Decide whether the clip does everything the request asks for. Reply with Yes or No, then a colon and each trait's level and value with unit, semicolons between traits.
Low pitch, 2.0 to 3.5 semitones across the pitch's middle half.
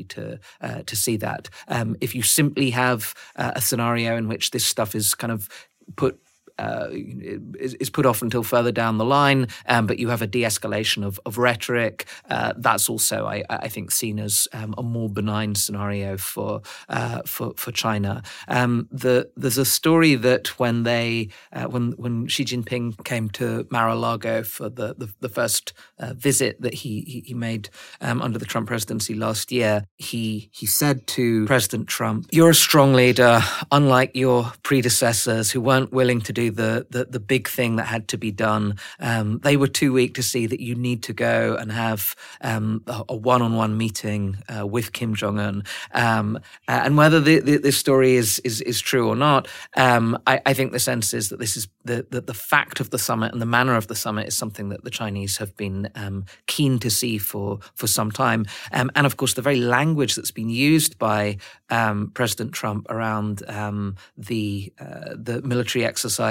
Yes: low, 115 Hz; narrow, 2.6 semitones